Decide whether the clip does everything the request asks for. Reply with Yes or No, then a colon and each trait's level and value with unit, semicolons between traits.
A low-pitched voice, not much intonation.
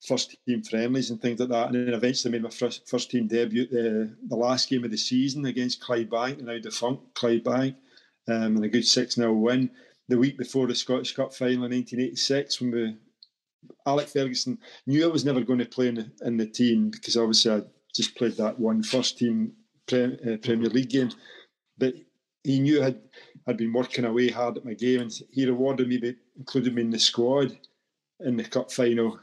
Yes: low, 125 Hz; narrow, 1.6 semitones